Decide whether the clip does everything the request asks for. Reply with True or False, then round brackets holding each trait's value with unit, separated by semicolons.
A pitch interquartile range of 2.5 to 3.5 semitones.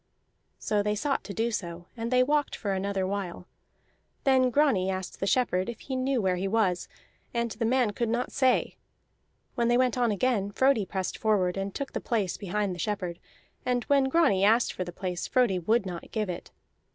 False (4.8 semitones)